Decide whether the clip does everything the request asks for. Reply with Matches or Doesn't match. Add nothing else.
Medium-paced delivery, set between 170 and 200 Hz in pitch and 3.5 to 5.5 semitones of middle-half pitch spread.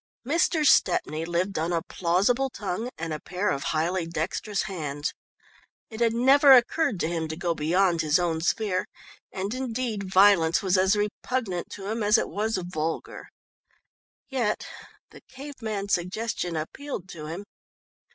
Matches